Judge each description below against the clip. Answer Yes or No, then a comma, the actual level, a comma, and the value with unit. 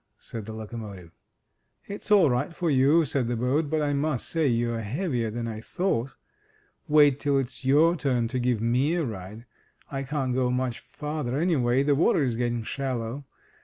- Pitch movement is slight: No, average, 4.0 semitones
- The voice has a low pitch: Yes, low, 130 Hz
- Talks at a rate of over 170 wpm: Yes, average, 180 wpm